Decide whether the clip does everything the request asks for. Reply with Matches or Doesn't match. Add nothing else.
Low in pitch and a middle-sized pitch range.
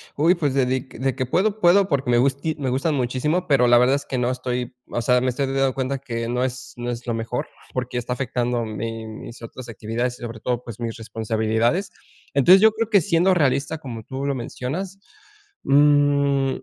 Matches